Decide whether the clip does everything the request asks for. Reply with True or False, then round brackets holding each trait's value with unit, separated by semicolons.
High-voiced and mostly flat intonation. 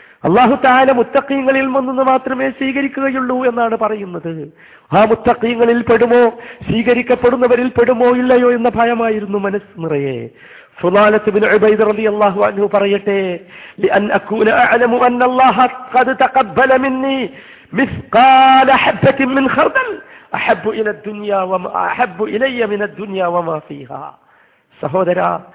False (235 Hz; 4.1 semitones)